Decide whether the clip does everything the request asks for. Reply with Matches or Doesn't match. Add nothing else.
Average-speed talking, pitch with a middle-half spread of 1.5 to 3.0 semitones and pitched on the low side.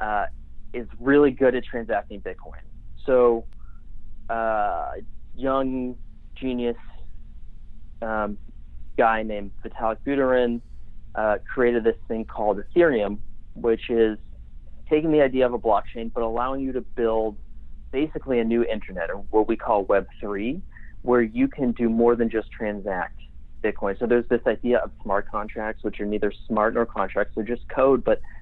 Matches